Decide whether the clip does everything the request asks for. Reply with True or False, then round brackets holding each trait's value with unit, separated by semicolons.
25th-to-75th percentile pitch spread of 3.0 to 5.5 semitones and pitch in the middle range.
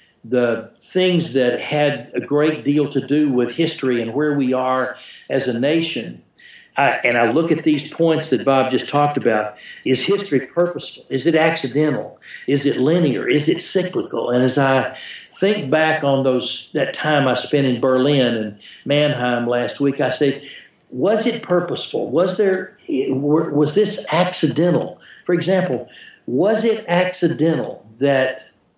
True (4.2 semitones; 145 Hz)